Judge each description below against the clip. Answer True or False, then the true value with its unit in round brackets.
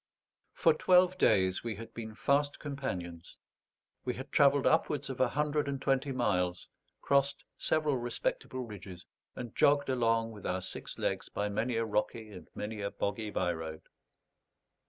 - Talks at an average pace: True (155 wpm)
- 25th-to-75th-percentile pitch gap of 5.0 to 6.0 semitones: True (5.5 semitones)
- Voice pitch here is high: False (115 Hz)